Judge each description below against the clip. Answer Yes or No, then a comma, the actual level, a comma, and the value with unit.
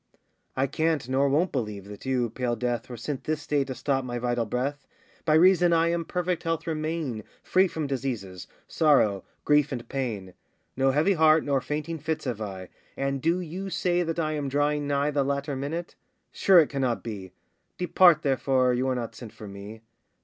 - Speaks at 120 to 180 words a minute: No, average, 190 wpm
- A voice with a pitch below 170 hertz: Yes, medium, 140 Hz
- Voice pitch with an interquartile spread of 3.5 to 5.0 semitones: Yes, average, 4.4 semitones